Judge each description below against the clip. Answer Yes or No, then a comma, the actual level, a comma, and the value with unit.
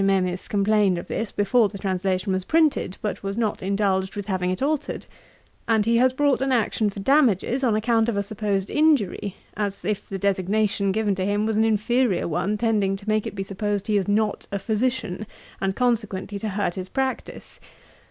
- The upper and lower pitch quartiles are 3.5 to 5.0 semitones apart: No, narrow, 2.5 semitones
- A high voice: Yes, high, 205 Hz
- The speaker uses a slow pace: No, average, 195 wpm